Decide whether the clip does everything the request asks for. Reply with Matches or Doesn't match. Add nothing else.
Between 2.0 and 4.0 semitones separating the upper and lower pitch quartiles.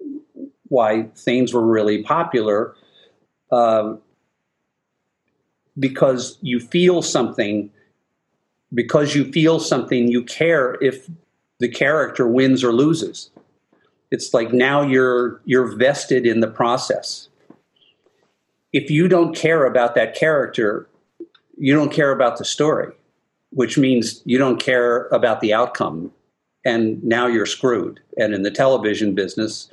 Doesn't match